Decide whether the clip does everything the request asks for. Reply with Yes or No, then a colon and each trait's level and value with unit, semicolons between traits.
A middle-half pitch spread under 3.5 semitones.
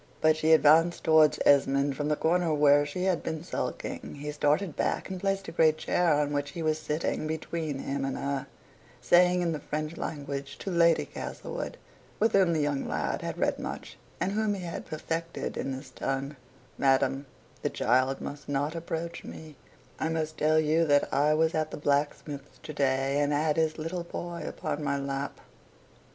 Yes: narrow, 2.6 semitones